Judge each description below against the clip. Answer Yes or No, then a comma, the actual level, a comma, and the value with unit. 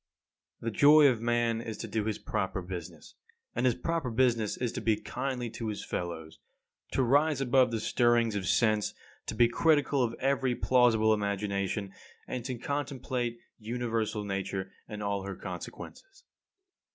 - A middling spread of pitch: Yes, average, 3.6 semitones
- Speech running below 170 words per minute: Yes, average, 160 wpm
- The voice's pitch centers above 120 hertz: No, low, 115 Hz